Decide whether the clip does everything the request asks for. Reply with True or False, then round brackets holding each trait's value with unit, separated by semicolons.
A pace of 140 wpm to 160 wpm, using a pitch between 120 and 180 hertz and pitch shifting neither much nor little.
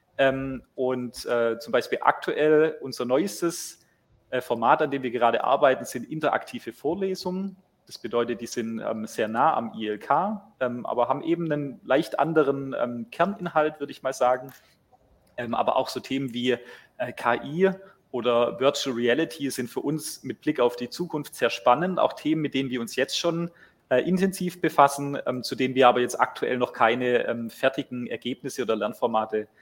True (150 wpm; 135 Hz; 4.1 semitones)